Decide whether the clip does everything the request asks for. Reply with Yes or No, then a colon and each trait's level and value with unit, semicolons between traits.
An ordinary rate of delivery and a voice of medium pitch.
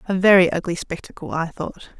Yes: average, 180 wpm; medium, 180 Hz